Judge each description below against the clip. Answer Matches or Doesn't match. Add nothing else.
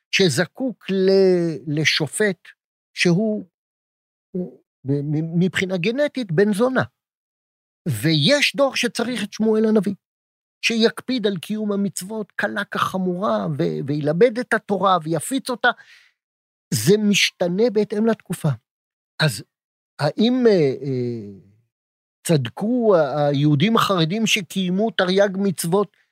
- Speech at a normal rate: Doesn't match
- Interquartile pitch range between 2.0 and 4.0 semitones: Doesn't match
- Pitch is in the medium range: Doesn't match